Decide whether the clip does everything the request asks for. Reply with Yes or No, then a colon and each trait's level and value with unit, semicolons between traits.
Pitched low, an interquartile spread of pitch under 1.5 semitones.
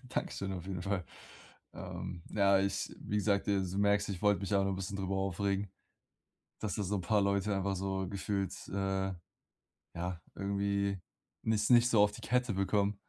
Yes: low, 100 Hz; narrow, 1.1 semitones